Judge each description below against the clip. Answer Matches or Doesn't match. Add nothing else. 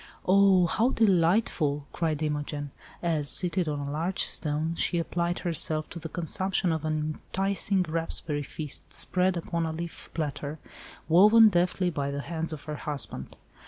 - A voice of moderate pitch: Matches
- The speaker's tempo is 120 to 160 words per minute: Matches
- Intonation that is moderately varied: Matches